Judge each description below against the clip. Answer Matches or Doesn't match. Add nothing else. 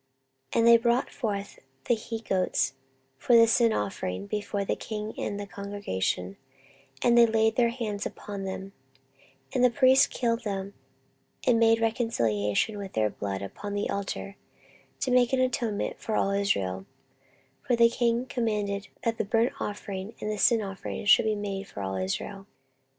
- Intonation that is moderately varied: Matches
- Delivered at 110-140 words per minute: Doesn't match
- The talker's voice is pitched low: Doesn't match